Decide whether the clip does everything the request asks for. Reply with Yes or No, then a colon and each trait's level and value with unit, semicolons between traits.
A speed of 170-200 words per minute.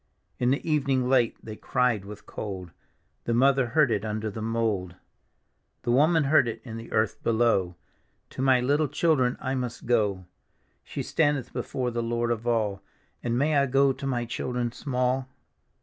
Yes: average, 180 wpm